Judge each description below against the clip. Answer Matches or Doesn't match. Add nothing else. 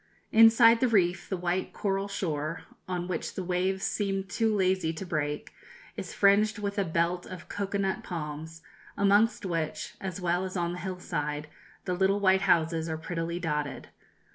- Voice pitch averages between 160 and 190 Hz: Matches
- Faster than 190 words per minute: Doesn't match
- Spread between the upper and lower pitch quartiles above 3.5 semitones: Doesn't match